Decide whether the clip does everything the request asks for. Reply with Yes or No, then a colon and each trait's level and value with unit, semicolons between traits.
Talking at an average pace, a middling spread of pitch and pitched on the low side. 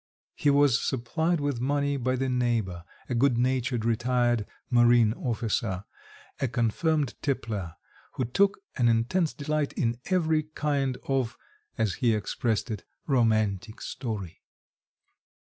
No: slow, 125 wpm; average, 3.7 semitones; low, 125 Hz